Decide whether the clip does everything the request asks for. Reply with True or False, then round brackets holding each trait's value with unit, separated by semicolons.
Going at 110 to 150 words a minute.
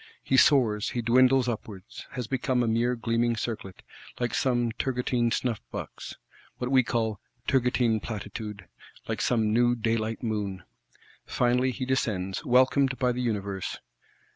True (135 wpm)